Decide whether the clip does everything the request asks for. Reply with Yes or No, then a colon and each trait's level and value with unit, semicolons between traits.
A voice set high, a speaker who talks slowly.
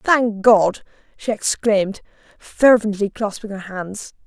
Yes: high, 210 Hz; slow, 115 wpm